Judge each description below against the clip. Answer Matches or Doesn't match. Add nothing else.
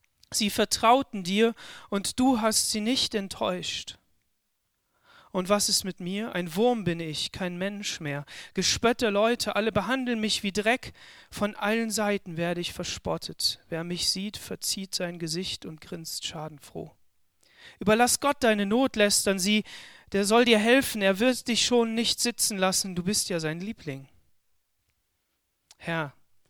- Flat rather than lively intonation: Doesn't match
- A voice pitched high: Matches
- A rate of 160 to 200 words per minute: Doesn't match